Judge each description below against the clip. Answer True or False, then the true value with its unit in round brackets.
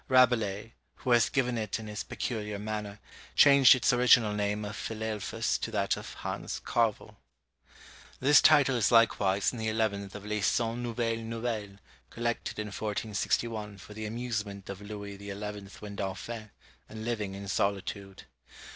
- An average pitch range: False (2.3 semitones)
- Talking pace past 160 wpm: False (150 wpm)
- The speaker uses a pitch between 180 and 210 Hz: False (110 Hz)